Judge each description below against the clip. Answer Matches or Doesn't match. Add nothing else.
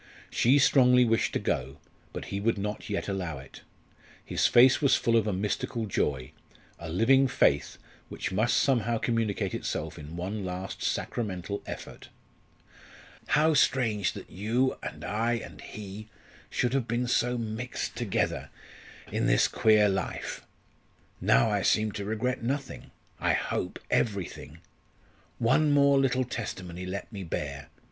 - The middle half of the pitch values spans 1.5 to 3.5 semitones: Doesn't match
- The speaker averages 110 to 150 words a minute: Matches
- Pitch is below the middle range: Matches